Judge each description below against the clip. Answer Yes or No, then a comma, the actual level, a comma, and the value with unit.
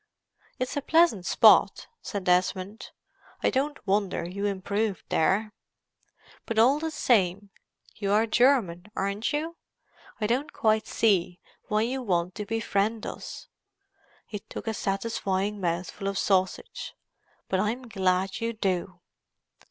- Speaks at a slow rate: Yes, slow, 130 wpm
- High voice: Yes, high, 205 Hz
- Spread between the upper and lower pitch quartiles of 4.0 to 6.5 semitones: No, average, 3.3 semitones